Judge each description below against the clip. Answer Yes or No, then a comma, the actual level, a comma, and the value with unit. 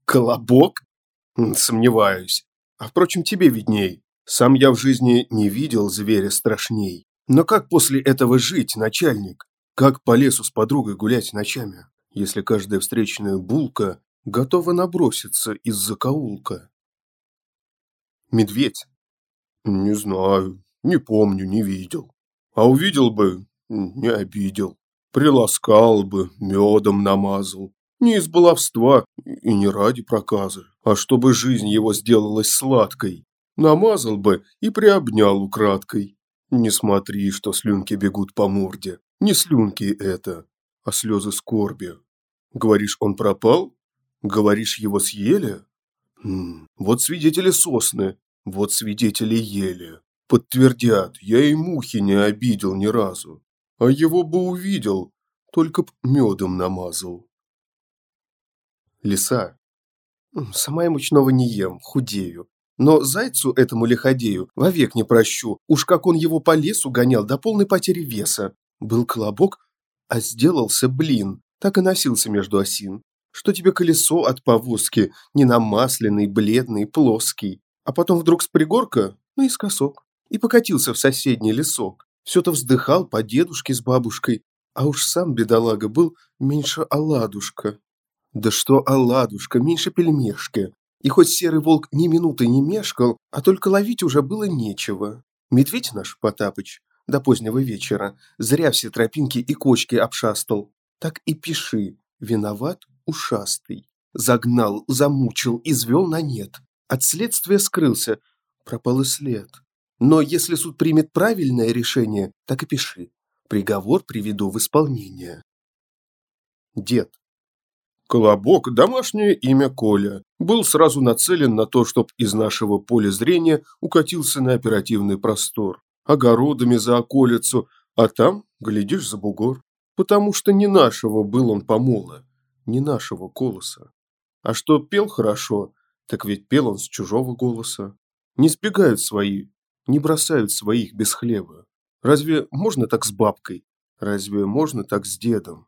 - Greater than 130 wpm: No, average, 125 wpm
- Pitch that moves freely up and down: Yes, wide, 6.3 semitones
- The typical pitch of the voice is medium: No, low, 120 Hz